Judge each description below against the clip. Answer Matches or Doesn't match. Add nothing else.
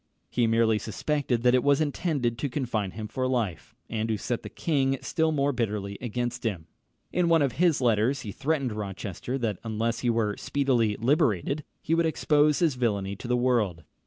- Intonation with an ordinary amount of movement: Matches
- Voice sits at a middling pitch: Doesn't match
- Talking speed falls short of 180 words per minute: Doesn't match